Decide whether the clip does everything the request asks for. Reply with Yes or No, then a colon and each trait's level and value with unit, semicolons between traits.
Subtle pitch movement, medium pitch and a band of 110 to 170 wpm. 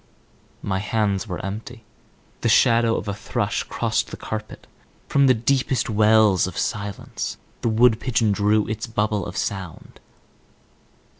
No: narrow, 2.2 semitones; low, 110 Hz; average, 140 wpm